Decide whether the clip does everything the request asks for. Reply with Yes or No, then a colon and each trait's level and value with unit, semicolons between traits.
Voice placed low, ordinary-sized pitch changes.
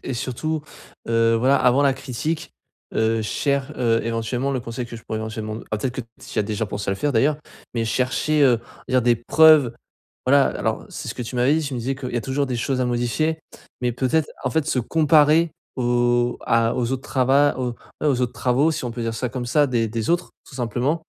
Yes: low, 125 Hz; average, 3.3 semitones